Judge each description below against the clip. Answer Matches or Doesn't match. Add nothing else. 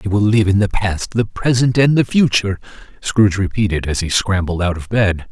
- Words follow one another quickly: Matches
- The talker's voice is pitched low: Matches